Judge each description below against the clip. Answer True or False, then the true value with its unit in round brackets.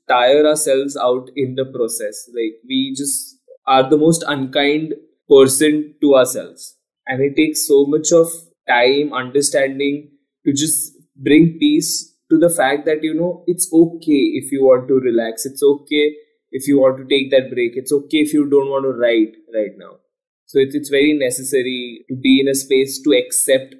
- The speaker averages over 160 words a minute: True (180 wpm)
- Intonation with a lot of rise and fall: False (3.5 semitones)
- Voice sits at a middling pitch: True (145 Hz)